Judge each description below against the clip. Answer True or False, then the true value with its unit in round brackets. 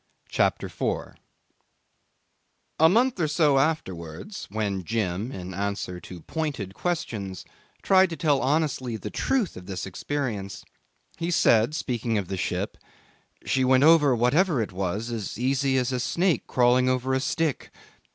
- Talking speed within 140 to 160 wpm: True (145 wpm)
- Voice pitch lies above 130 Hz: False (125 Hz)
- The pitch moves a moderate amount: False (7.3 semitones)